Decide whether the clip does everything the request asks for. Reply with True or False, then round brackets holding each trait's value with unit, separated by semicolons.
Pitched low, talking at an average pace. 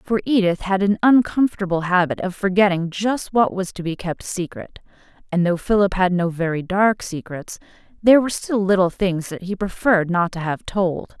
False (190 Hz; 190 wpm)